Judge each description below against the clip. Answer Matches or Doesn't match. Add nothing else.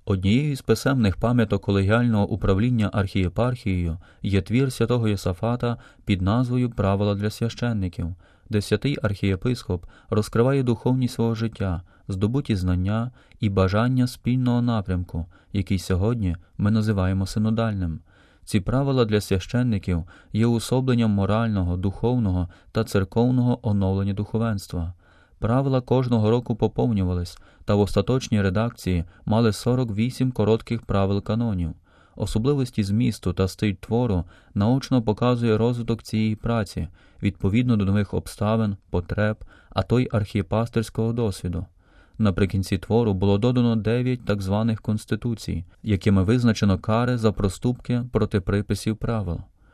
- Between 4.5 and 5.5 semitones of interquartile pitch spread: Doesn't match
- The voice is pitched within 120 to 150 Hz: Doesn't match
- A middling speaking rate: Matches